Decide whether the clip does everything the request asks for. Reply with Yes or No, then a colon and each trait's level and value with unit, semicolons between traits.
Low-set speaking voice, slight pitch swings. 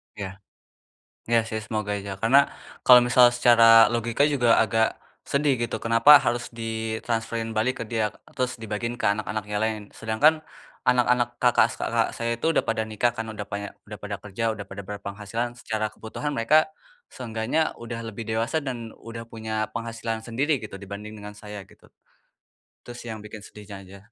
Yes: low, 115 Hz; narrow, 2.1 semitones